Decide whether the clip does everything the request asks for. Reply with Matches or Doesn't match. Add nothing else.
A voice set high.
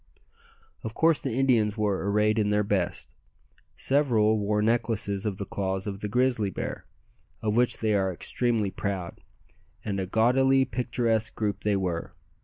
Doesn't match